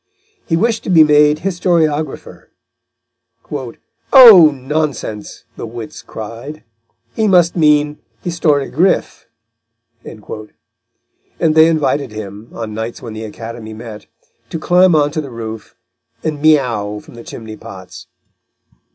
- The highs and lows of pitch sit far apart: Yes, wide, 6.2 semitones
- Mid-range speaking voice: Yes, medium, 145 Hz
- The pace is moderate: No, slow, 115 wpm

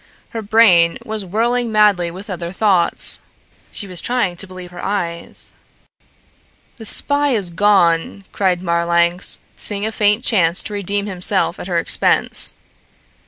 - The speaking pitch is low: No, high, 195 Hz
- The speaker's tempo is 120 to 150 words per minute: Yes, average, 140 wpm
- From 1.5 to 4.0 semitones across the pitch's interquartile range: Yes, average, 3.4 semitones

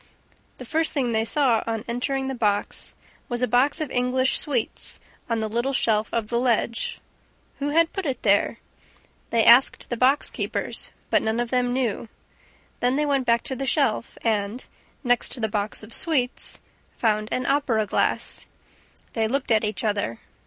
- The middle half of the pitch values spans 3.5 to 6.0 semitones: No, average, 3.1 semitones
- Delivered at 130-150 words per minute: No, average, 175 wpm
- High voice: Yes, high, 240 Hz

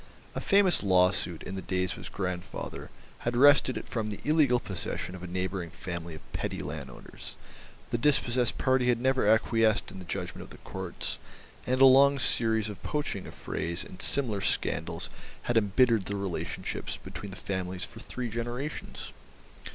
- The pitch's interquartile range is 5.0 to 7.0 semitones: Yes, average, 5.3 semitones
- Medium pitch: No, low, 105 Hz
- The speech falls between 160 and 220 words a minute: Yes, average, 170 wpm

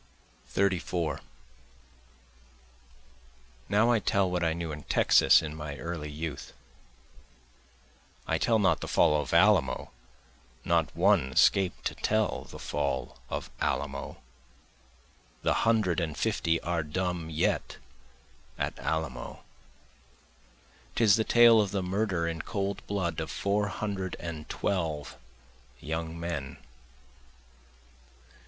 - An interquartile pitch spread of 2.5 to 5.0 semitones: Yes, average, 4.2 semitones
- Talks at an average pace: No, slow, 115 wpm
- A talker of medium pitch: No, very low, 85 Hz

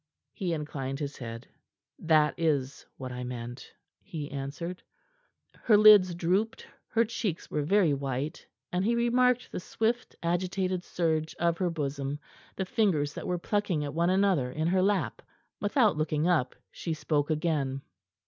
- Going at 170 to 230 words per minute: No, average, 150 wpm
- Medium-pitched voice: Yes, medium, 165 Hz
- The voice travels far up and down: No, average, 4.9 semitones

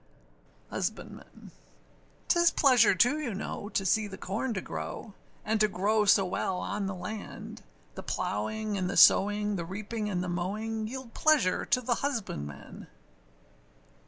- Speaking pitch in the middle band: No, high, 210 Hz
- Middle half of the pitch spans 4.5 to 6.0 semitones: No, average, 2.9 semitones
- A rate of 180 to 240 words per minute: No, average, 150 wpm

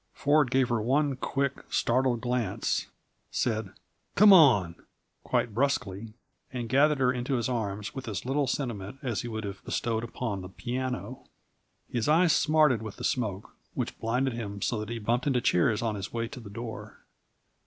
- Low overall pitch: Yes, low, 120 Hz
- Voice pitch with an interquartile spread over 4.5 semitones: No, average, 3.4 semitones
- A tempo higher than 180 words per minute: No, average, 175 wpm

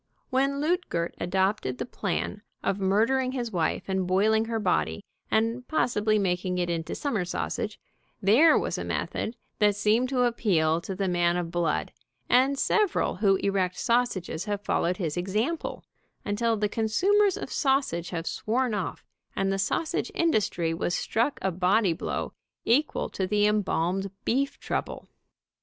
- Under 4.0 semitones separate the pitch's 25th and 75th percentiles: No, average, 5.1 semitones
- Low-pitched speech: No, high, 205 Hz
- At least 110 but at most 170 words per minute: Yes, average, 155 wpm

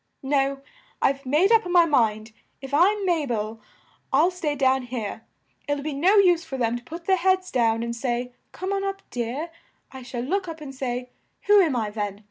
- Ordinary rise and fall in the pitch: No, wide, 6.3 semitones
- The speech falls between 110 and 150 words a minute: No, average, 195 wpm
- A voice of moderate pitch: No, very high, 275 Hz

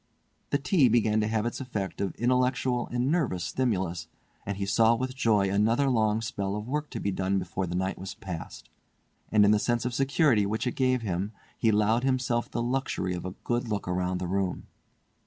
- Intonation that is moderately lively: Yes, average, 4.3 semitones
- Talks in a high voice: No, low, 110 Hz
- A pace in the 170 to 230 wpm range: Yes, average, 200 wpm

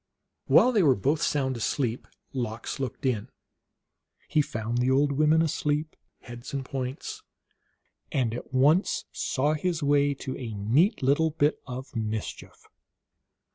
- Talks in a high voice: No, low, 135 Hz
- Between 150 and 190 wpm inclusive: No, slow, 135 wpm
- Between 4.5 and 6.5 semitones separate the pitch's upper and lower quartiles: No, average, 3.6 semitones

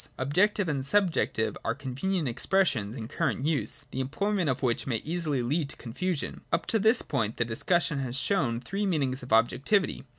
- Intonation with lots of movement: Yes, wide, 6.9 semitones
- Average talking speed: Yes, average, 175 wpm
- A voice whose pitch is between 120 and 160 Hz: Yes, medium, 140 Hz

